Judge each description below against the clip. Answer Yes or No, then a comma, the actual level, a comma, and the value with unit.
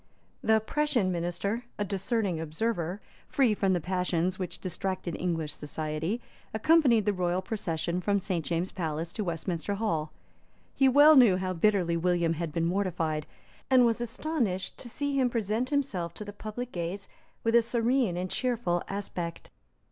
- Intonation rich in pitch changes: No, average, 5.0 semitones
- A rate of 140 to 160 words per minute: Yes, average, 155 wpm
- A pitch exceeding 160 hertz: Yes, high, 190 Hz